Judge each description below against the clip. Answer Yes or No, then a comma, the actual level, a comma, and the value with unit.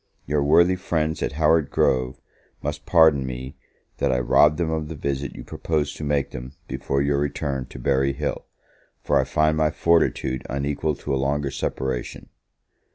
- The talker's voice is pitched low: Yes, very low, 70 Hz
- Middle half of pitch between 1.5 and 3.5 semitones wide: Yes, narrow, 2.4 semitones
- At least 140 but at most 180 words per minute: Yes, average, 170 wpm